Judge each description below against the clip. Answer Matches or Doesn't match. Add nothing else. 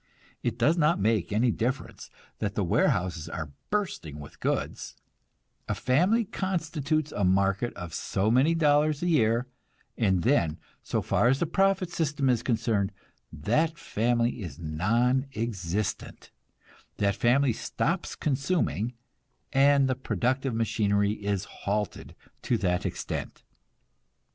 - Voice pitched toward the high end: Doesn't match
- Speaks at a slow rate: Matches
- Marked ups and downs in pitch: Matches